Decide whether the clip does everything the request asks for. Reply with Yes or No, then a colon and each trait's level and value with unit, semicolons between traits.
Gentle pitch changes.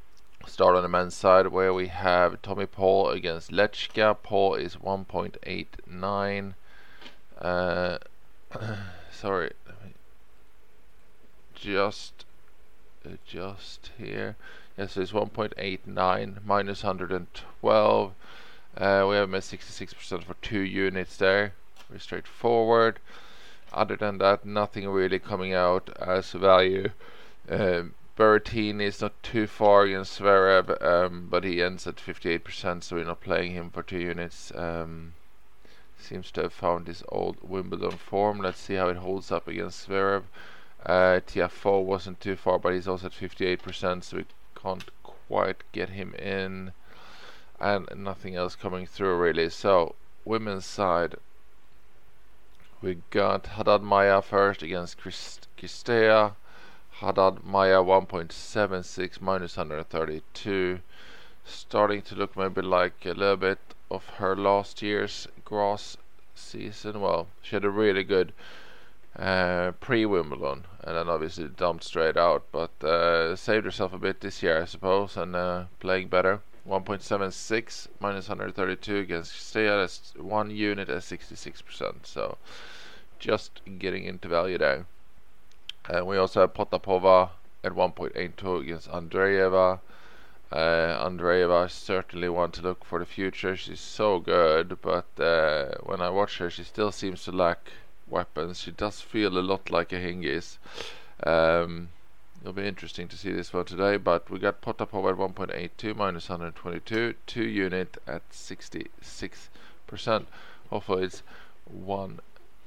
Yes: narrow, 2.0 semitones